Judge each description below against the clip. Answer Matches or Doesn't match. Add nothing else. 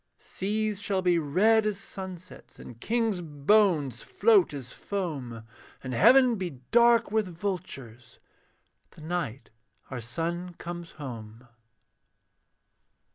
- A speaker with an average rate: Doesn't match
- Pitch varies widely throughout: Matches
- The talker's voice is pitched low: Doesn't match